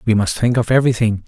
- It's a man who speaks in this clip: Yes, male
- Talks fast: Yes, fast, 235 wpm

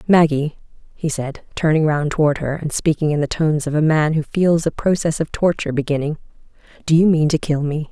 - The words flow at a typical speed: No, fast, 210 wpm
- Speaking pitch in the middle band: Yes, medium, 155 Hz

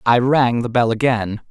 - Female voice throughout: No, male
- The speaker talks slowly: No, average, 200 wpm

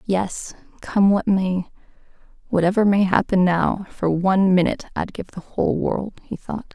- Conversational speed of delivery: Yes, average, 150 wpm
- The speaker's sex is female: Yes, female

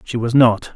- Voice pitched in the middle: No, low, 120 Hz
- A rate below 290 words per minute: Yes, fast, 240 wpm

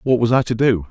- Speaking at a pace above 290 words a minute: Yes, fast, 335 wpm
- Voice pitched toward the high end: No, low, 115 Hz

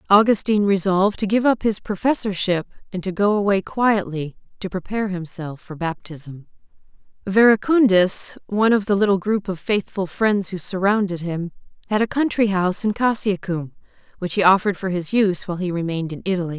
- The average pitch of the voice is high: Yes, high, 195 Hz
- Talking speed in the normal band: Yes, average, 165 wpm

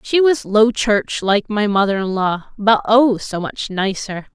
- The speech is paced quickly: No, average, 195 wpm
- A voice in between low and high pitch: No, high, 210 Hz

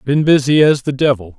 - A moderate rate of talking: No, fast, 215 wpm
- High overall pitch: No, low, 135 Hz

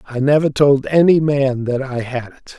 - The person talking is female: No, male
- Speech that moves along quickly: Yes, fast, 210 wpm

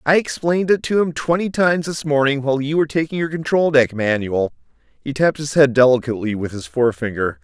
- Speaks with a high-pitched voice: No, medium, 140 Hz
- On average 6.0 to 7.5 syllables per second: Yes, 6.2 syllables/s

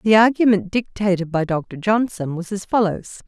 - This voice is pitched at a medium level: No, high, 200 Hz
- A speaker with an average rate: Yes, average, 165 wpm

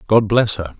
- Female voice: No, male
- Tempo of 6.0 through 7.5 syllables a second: No, 4.8 syllables/s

